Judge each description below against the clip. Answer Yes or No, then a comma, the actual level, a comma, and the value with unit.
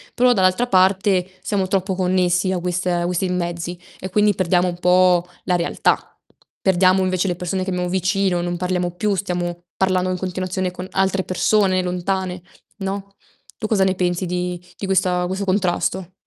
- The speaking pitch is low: No, medium, 185 Hz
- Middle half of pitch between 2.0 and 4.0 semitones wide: No, narrow, 1.1 semitones